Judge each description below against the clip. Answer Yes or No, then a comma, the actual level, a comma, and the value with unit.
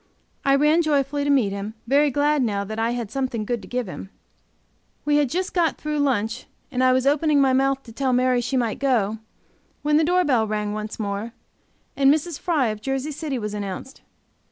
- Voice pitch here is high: Yes, very high, 260 Hz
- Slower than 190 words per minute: No, fast, 205 wpm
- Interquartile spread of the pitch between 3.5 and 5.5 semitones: Yes, average, 4.7 semitones